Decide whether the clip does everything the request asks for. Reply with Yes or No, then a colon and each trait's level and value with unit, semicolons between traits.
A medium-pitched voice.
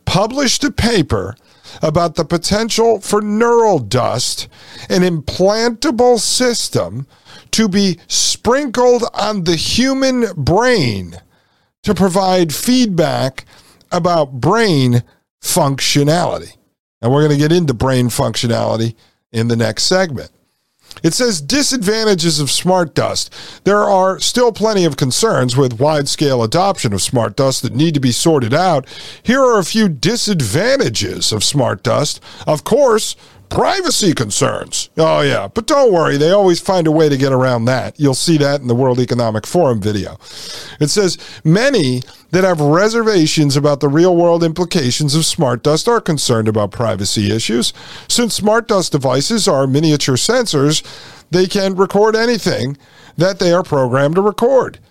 Yes: medium, 160 Hz